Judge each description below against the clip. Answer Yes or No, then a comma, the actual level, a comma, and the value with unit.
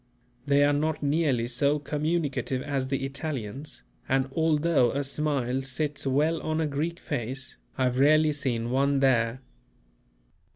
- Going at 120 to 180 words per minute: Yes, average, 140 wpm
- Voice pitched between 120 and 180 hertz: Yes, medium, 140 Hz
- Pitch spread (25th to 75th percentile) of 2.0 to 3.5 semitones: Yes, narrow, 2.6 semitones